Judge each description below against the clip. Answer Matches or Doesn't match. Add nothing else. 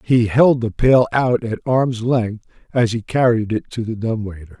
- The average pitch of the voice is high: Doesn't match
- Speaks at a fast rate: Matches